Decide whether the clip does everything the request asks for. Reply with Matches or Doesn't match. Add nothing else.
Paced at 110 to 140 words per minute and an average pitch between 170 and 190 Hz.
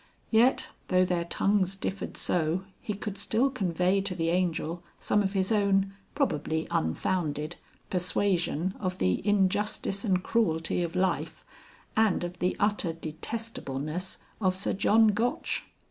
Matches